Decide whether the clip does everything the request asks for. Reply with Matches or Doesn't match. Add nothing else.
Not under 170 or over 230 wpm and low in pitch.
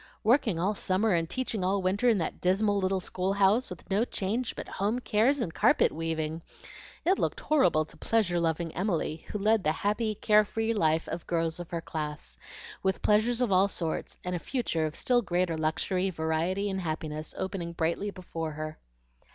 Doesn't match